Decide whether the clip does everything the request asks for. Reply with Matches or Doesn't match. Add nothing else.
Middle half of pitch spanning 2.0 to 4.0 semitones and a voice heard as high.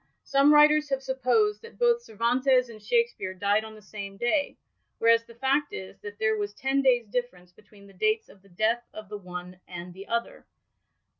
Doesn't match